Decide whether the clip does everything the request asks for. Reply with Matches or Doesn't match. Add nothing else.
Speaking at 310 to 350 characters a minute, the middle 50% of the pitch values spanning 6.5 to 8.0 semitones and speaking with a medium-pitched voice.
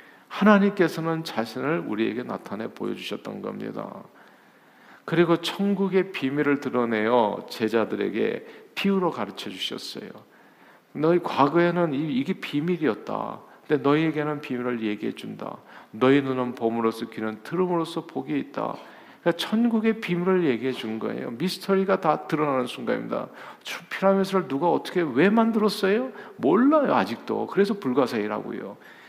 Matches